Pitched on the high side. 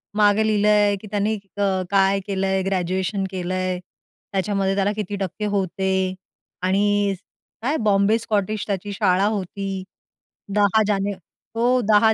Yes: high, 200 Hz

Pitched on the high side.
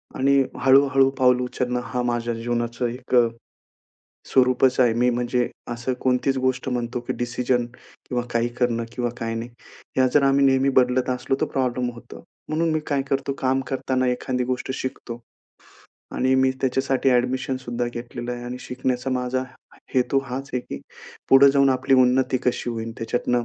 No: low, 125 Hz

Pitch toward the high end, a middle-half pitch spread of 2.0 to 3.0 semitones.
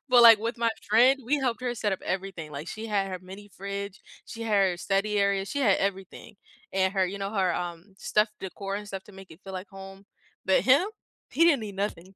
Yes: high, 200 Hz; narrow, 2.4 semitones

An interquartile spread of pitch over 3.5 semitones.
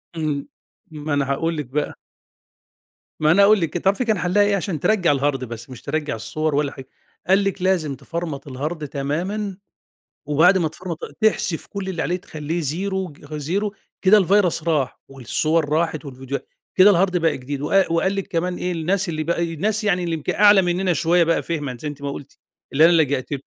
Yes: average, 4.2 semitones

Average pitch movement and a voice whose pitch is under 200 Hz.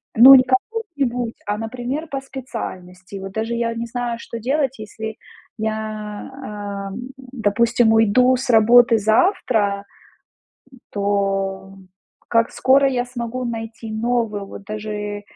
No: average, 3.4 semitones; high, 230 Hz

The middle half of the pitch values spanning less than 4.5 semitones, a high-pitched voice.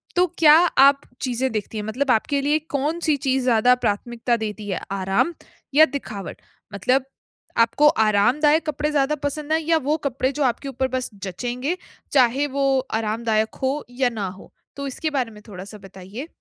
No: average, 4.8 semitones; very high, 255 Hz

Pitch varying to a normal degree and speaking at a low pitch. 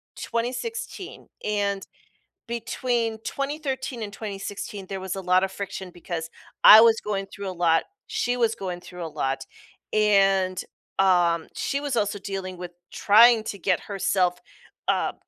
No: average, 3.7 semitones; high, 200 Hz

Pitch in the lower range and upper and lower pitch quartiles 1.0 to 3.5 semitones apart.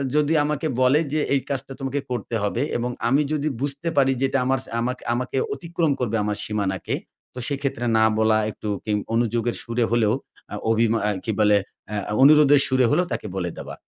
No: low, 125 Hz; average, 4.0 semitones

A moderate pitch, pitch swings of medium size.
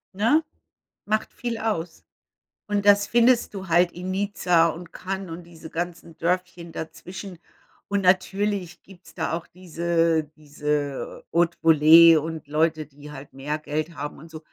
Yes: medium, 170 Hz; average, 3.1 semitones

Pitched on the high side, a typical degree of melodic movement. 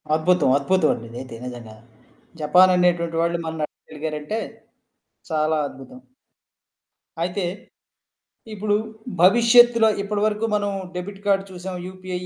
No: medium, 180 Hz; average, 4.5 semitones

